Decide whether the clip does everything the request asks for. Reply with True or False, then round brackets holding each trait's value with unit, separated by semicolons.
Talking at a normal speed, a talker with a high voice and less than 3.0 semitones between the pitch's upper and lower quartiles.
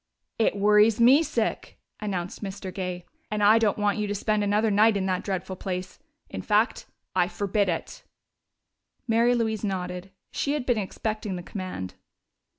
True (160 wpm; 205 Hz; 2.6 semitones)